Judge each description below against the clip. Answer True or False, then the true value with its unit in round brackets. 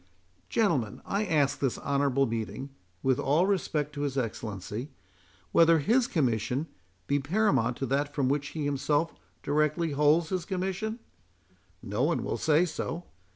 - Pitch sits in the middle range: True (145 Hz)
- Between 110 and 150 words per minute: True (145 wpm)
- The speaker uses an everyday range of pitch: True (3.8 semitones)